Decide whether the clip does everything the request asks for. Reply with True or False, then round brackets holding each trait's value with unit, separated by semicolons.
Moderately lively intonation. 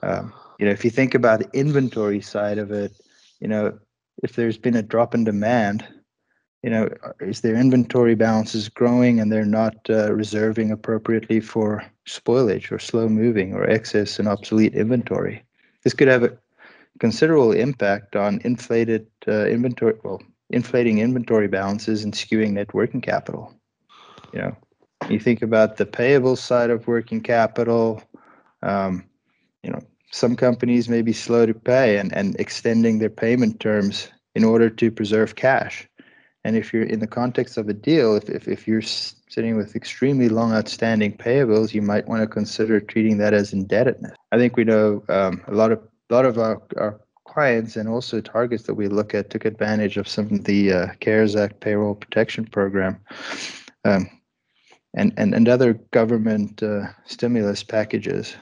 False (1.9 semitones)